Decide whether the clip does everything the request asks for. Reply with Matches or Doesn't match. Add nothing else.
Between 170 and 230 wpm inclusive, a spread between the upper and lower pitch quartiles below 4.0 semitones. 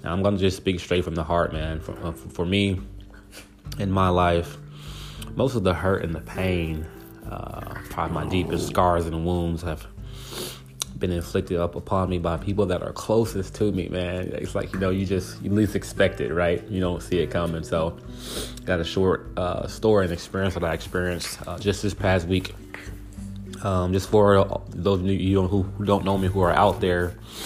Matches